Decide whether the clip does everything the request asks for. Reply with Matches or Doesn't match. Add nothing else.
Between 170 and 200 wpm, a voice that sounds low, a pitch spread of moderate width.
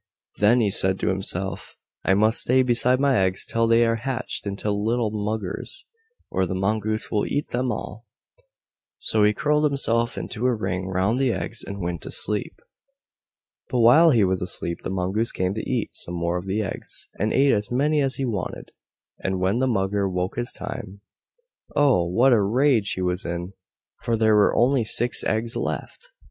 Matches